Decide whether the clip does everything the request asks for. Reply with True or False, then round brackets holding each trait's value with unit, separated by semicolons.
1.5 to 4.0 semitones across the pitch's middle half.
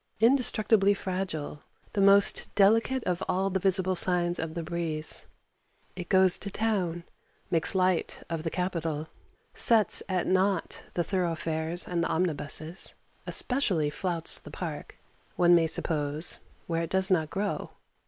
True (2.9 semitones)